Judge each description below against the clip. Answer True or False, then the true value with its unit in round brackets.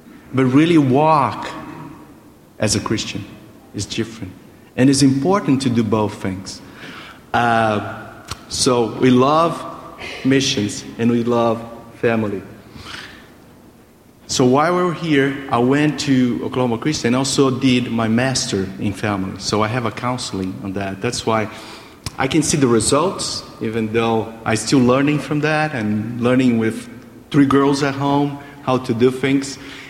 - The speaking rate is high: False (145 wpm)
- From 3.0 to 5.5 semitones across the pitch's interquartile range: True (3.6 semitones)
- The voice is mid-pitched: False (125 Hz)